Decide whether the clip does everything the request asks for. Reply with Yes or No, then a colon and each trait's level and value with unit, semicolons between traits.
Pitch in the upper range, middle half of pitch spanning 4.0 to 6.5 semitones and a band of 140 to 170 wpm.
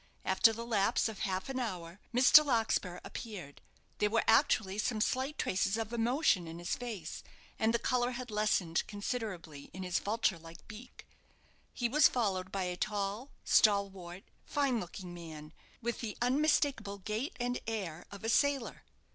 Yes: high, 215 Hz; average, 4.5 semitones; average, 160 wpm